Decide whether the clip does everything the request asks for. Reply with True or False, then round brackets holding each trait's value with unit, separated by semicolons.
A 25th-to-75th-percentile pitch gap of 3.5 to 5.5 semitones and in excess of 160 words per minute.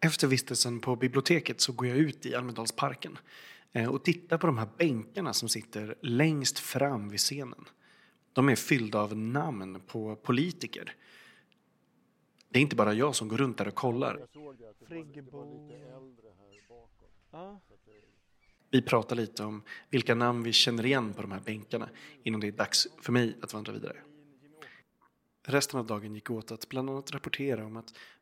False (4.3 semitones; 155 wpm)